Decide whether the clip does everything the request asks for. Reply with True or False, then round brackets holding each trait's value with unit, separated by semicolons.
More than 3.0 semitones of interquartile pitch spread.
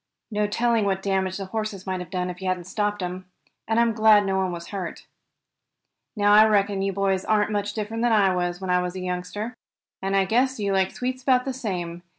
False (2.7 semitones)